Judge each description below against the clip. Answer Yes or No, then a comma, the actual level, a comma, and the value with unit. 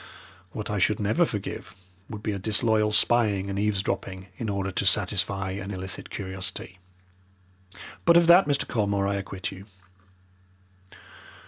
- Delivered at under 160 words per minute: Yes, average, 140 wpm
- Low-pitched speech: Yes, low, 100 Hz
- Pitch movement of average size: No, narrow, 2.0 semitones